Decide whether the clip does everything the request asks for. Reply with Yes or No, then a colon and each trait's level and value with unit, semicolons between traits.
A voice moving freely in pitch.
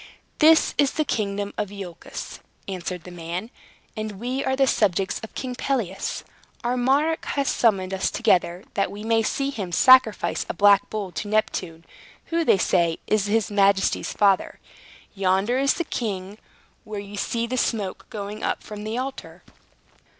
No: average, 4.2 semitones